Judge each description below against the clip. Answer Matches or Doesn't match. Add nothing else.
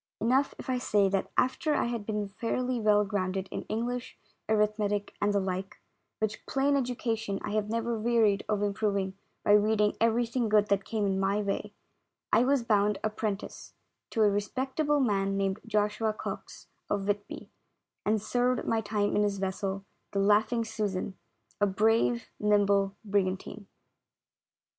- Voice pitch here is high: Matches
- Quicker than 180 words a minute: Doesn't match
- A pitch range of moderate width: Doesn't match